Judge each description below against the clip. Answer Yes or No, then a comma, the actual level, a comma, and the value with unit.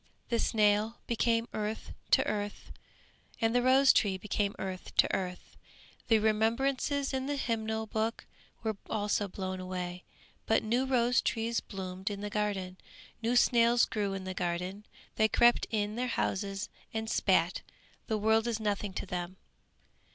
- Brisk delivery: No, average, 150 wpm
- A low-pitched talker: No, high, 215 Hz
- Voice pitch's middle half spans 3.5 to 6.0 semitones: No, average, 2.9 semitones